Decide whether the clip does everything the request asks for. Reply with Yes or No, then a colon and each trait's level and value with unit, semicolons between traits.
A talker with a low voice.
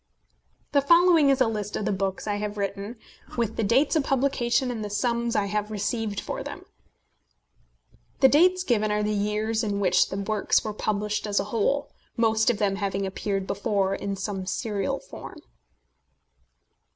No: high, 210 Hz